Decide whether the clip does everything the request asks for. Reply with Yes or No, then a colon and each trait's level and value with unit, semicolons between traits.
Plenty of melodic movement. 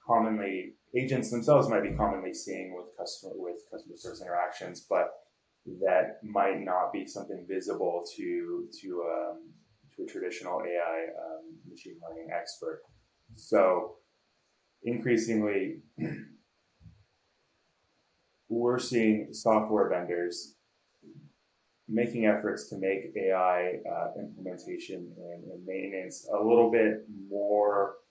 Yes: wide, 7.4 semitones